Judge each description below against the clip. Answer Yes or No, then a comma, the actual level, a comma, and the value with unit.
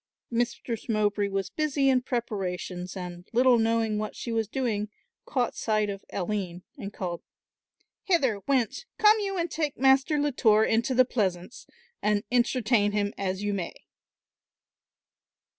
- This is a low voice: No, high, 225 Hz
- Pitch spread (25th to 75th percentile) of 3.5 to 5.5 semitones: Yes, average, 4.3 semitones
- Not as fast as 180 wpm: Yes, average, 140 wpm